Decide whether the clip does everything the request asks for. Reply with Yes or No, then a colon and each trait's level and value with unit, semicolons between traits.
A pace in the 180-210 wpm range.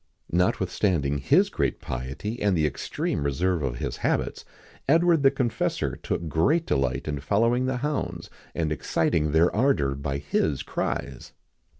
No: average, 155 wpm